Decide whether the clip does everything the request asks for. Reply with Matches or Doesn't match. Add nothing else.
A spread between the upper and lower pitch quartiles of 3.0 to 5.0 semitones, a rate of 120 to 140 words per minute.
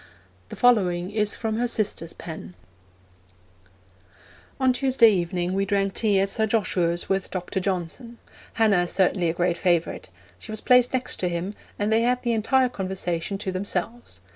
Doesn't match